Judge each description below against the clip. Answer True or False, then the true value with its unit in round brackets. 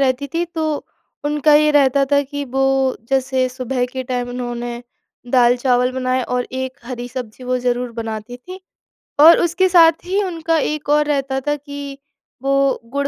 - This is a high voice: True (265 Hz)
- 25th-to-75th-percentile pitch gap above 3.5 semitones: False (2.8 semitones)